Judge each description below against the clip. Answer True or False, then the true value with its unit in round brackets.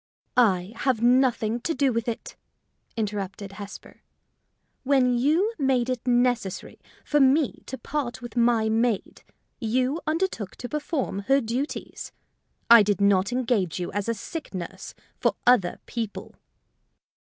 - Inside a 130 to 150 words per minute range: True (135 wpm)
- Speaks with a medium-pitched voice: False (240 Hz)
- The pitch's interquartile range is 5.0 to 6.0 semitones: False (4.1 semitones)